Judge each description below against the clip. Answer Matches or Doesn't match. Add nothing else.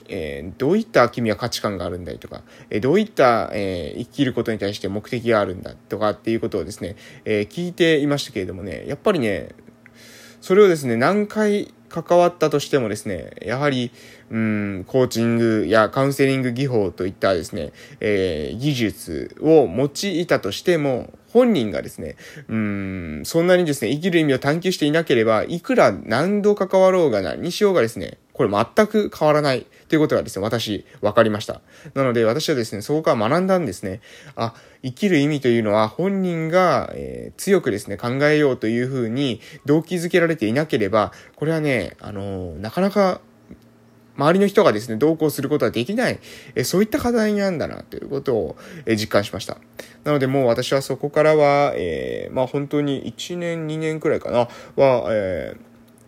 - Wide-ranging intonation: Matches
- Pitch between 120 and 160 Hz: Matches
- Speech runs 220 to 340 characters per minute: Doesn't match